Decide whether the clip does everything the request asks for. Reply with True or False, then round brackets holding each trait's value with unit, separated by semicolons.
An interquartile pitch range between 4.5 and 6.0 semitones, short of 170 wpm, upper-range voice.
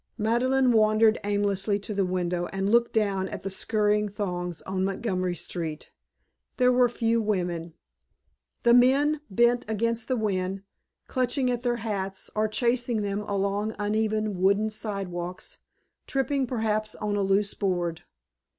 False (3.2 semitones; 140 wpm; 210 Hz)